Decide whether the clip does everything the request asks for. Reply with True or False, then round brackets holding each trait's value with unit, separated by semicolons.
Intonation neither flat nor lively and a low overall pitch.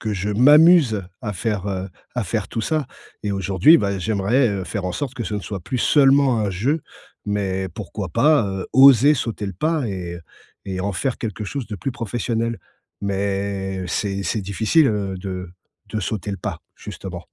True (4.2 semitones; 105 Hz)